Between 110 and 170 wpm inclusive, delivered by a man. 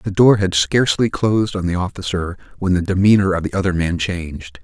No: fast, 205 wpm; male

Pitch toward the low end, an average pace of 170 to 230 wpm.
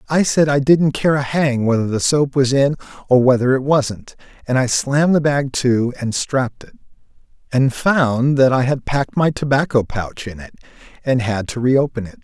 Yes: low, 130 Hz; average, 200 wpm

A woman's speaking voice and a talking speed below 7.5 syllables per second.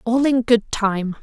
Yes: female; 3.7 syllables/s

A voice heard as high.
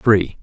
No: very low, 95 Hz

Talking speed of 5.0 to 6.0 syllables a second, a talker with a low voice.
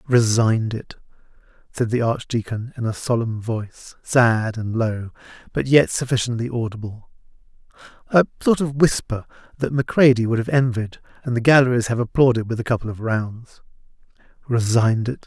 Yes: 5.2 syllables/s; low, 120 Hz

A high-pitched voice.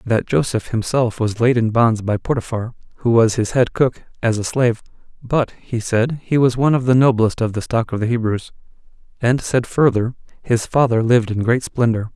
No: low, 120 Hz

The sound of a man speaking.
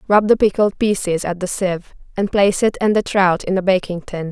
No: female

